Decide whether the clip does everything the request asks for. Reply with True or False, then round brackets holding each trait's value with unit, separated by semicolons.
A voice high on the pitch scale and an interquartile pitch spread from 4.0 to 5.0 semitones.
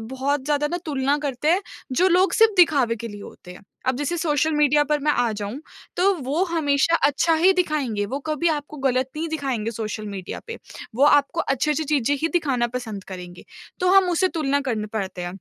True (285 Hz; 4.7 semitones)